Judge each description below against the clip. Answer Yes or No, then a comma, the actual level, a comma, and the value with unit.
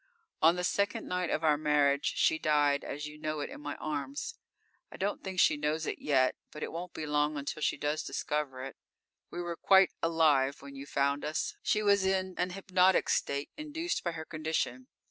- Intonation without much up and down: No, average, 3.8 semitones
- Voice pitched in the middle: Yes, medium, 155 Hz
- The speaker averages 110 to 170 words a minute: No, fast, 205 wpm